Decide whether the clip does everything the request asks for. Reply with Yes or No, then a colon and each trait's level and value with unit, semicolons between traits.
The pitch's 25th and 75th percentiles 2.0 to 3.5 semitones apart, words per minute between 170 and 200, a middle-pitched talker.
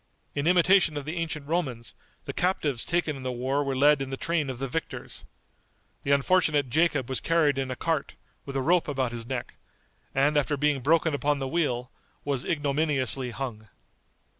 Yes: average, 3.2 semitones; average, 185 wpm; medium, 145 Hz